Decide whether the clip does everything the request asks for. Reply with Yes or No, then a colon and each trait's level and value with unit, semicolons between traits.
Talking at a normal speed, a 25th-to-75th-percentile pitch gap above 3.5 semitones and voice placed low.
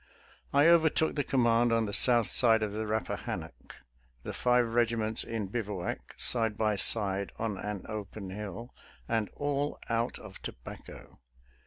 No: average, 165 wpm; narrow, 2.4 semitones; low, 110 Hz